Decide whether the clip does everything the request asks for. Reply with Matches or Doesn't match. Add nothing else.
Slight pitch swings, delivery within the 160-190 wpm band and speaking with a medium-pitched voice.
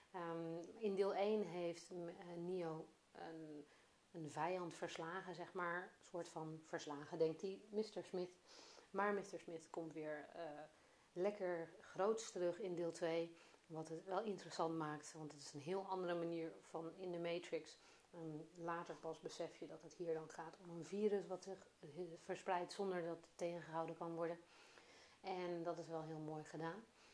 Matches